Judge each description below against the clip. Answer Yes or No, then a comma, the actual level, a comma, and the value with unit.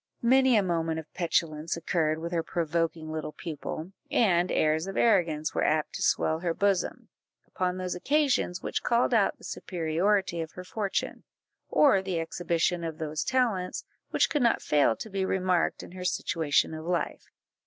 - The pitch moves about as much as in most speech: Yes, average, 3.3 semitones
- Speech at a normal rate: Yes, average, 170 wpm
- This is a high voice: No, medium, 175 Hz